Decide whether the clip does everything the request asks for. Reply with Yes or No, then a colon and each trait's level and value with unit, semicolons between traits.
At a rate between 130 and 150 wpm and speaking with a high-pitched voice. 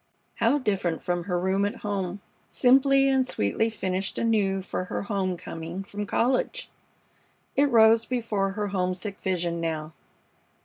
Yes: average, 140 wpm; high, 200 Hz